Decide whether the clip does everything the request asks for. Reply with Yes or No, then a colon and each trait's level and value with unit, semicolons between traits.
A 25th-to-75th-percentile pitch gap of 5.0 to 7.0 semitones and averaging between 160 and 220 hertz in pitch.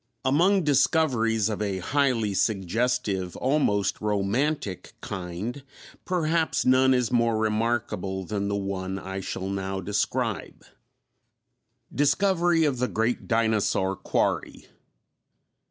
No: wide, 5.4 semitones; low, 110 Hz